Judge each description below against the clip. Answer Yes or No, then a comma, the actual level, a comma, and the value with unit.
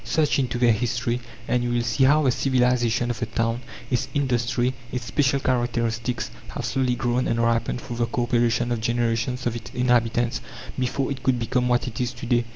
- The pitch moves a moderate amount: No, narrow, 1.2 semitones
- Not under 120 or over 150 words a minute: No, average, 200 wpm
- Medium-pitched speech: No, low, 120 Hz